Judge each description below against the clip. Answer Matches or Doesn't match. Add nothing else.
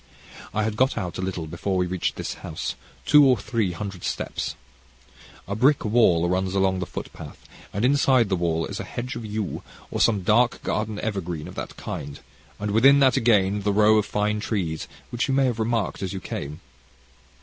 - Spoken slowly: Doesn't match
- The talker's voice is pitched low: Matches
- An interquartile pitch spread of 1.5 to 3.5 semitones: Doesn't match